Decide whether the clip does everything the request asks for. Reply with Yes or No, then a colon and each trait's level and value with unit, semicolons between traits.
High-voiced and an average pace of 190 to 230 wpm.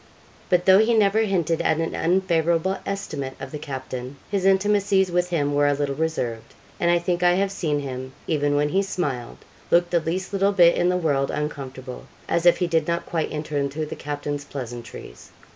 No: medium, 165 Hz; average, 195 wpm